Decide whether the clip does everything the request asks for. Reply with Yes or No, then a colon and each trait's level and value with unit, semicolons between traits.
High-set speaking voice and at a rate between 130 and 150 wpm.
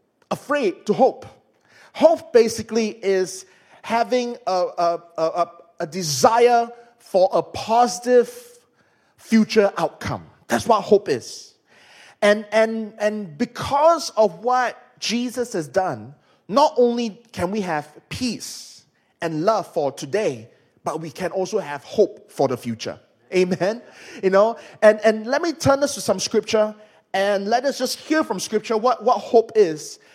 Yes: high, 215 Hz; average, 145 wpm